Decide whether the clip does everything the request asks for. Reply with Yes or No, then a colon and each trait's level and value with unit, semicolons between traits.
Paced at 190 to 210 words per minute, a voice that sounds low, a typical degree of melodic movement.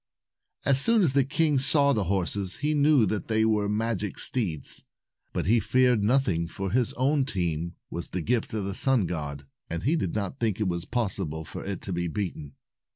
No: average, 200 wpm; low, 105 Hz; wide, 6.7 semitones